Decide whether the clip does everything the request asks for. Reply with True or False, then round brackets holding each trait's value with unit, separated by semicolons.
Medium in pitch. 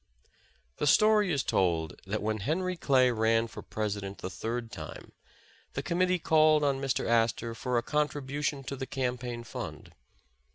False (125 Hz)